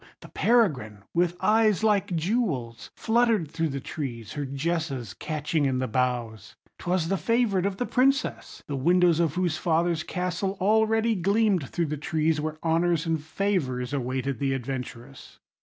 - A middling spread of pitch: No, wide, 6.2 semitones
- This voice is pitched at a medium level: Yes, medium, 165 Hz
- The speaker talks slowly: No, average, 155 wpm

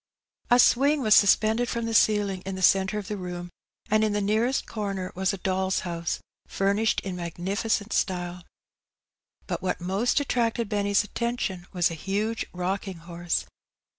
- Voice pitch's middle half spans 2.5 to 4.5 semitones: Yes, average, 3.1 semitones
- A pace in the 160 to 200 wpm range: Yes, average, 165 wpm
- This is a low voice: No, high, 200 Hz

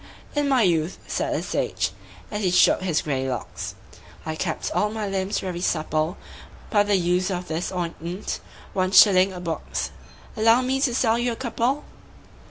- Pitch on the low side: No, high, 190 Hz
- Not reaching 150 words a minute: No, average, 175 wpm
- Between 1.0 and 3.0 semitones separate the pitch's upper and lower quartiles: No, average, 4.6 semitones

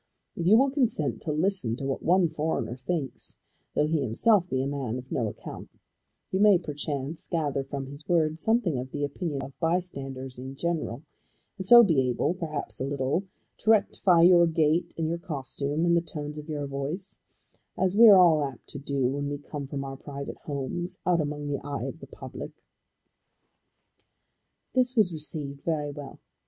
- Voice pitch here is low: No, medium, 150 Hz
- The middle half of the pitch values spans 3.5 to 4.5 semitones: Yes, average, 4.0 semitones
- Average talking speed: Yes, average, 185 wpm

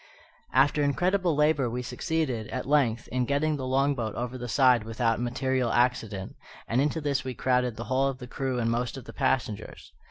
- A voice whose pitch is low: Yes, low, 130 Hz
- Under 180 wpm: No, average, 195 wpm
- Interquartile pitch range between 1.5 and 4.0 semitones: Yes, narrow, 2.6 semitones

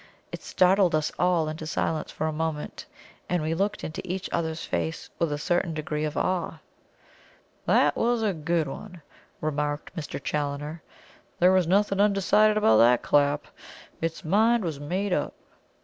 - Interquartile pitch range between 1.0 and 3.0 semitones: No, average, 3.7 semitones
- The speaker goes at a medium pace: Yes, average, 160 wpm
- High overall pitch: No, medium, 165 Hz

